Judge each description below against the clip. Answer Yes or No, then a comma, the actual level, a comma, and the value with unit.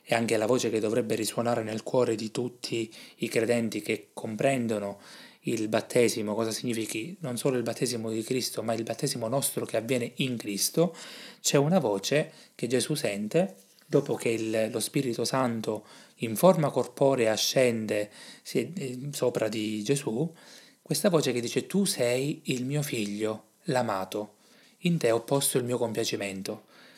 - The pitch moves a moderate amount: Yes, average, 4.3 semitones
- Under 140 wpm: No, average, 155 wpm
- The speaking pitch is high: No, low, 120 Hz